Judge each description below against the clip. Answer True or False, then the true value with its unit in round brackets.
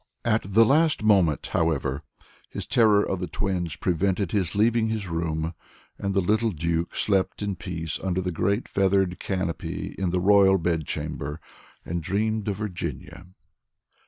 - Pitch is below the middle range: True (95 Hz)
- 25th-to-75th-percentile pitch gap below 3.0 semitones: False (3.5 semitones)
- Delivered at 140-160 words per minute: True (150 wpm)